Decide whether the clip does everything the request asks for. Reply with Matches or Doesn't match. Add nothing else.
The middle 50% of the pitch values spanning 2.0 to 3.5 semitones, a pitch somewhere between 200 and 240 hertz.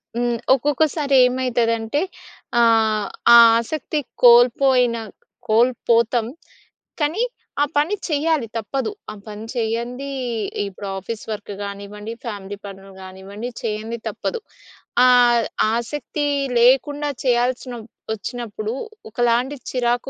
Matches